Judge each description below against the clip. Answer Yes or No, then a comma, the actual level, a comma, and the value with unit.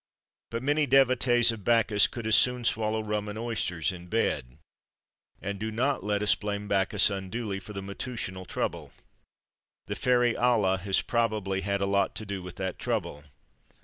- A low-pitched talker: Yes, low, 105 Hz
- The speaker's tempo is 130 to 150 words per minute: No, average, 170 wpm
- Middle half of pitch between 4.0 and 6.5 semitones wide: No, average, 3.3 semitones